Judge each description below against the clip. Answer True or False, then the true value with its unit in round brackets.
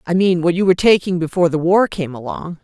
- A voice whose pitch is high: False (175 Hz)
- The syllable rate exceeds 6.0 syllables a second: True (6.4 syllables/s)